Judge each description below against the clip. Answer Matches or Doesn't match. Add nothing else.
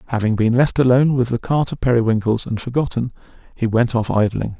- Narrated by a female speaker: Doesn't match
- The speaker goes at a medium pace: Matches